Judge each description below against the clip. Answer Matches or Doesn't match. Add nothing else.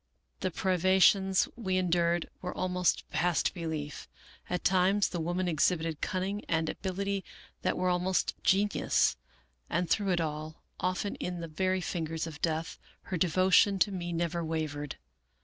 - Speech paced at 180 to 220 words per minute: Doesn't match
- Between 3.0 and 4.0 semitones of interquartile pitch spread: Doesn't match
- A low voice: Doesn't match